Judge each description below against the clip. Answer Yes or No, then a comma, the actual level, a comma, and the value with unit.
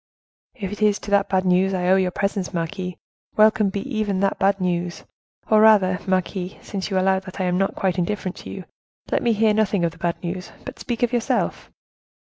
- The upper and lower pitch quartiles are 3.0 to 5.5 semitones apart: No, narrow, 2.4 semitones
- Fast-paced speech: Yes, fast, 215 wpm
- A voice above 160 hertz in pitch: Yes, high, 190 Hz